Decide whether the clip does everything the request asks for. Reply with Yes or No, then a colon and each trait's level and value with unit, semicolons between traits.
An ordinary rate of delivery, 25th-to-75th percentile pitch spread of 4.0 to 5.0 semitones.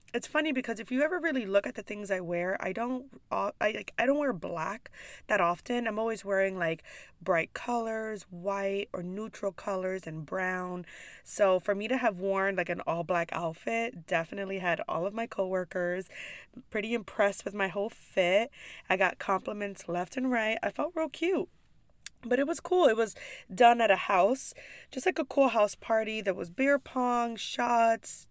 Yes: average, 190 wpm; average, 4.4 semitones